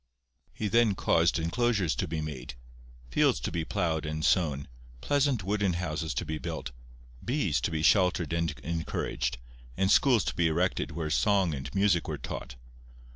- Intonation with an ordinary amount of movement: Yes, average, 4.0 semitones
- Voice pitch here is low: Yes, very low, 85 Hz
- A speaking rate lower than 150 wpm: No, average, 165 wpm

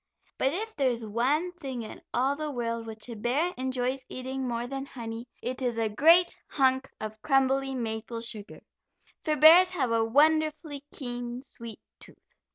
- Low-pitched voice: No, very high, 260 Hz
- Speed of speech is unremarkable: Yes, average, 165 wpm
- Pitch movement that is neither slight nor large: Yes, average, 3.6 semitones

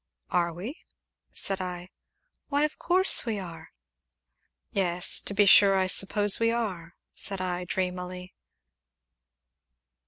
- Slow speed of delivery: Yes, slow, 120 wpm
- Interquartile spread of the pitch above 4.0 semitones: No, narrow, 2.5 semitones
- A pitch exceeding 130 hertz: Yes, high, 190 Hz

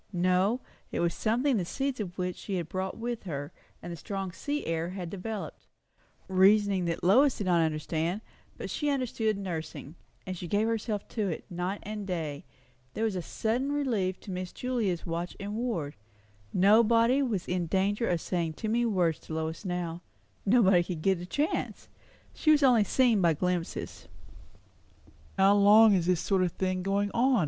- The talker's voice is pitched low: No, high, 195 Hz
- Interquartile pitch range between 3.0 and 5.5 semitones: Yes, average, 4.2 semitones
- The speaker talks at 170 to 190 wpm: Yes, average, 180 wpm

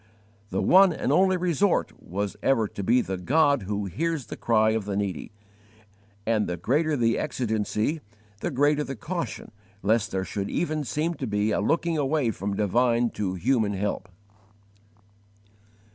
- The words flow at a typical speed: Yes, average, 160 wpm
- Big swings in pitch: Yes, wide, 6.6 semitones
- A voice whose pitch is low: Yes, low, 115 Hz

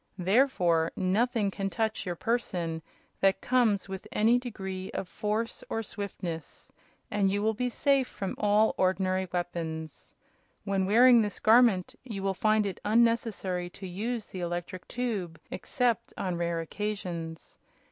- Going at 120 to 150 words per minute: Yes, average, 140 wpm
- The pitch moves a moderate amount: Yes, average, 3.8 semitones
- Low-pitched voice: No, high, 195 Hz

